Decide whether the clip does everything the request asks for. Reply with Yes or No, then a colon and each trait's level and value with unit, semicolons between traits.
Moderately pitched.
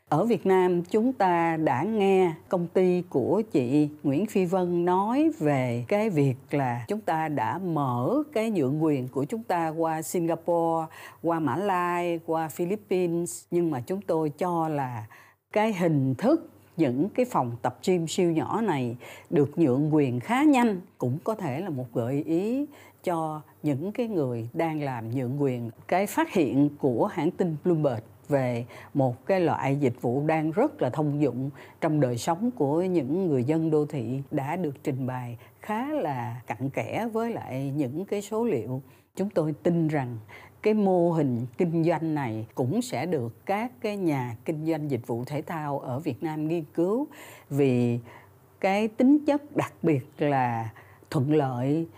Yes: medium, 155 Hz